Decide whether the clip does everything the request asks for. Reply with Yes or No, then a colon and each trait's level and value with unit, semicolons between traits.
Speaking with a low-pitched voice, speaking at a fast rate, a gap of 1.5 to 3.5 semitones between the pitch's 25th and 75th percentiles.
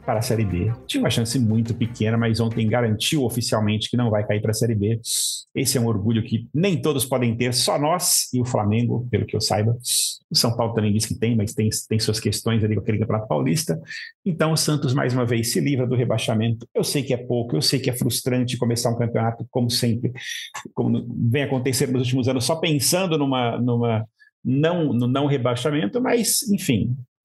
Yes: low, 120 Hz; fast, 215 wpm; average, 2.8 semitones